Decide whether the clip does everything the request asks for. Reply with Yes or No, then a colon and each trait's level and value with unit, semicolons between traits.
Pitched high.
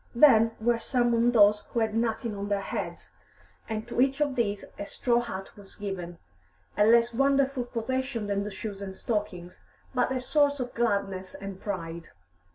Yes: high, 225 Hz